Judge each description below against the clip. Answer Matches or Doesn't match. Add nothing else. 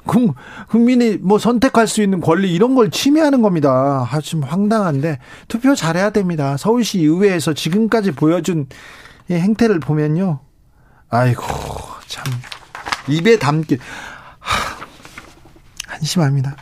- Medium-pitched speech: Matches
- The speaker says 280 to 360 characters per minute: Doesn't match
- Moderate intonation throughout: Doesn't match